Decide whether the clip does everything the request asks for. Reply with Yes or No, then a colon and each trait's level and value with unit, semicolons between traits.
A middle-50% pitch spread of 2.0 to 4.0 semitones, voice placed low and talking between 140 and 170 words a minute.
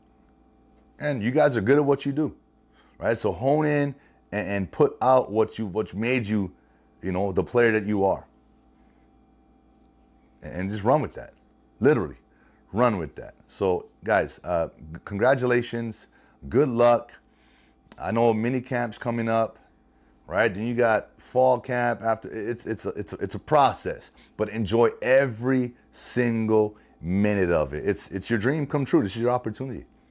Yes: average, 3.3 semitones; low, 115 Hz; average, 165 wpm